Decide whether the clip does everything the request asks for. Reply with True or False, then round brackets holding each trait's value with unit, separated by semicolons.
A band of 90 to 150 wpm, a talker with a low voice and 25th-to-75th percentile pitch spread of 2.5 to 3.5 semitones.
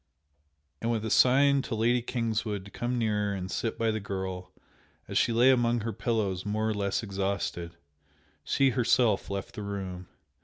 False (170 wpm; 110 Hz; 3.1 semitones)